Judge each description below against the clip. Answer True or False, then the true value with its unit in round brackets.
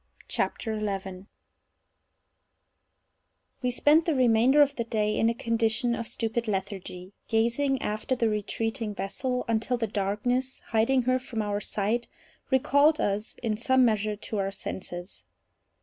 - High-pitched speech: True (225 Hz)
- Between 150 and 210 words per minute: False (135 wpm)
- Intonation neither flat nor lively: True (3.1 semitones)